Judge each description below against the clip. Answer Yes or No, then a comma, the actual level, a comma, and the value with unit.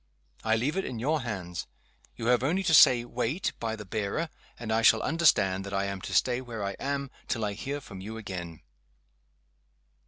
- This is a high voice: No, low, 115 Hz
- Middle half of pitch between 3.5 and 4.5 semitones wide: No, wide, 5.6 semitones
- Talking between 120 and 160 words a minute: No, average, 195 wpm